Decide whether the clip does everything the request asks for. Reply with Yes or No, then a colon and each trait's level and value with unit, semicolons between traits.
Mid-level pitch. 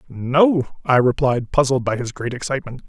No: low, 130 Hz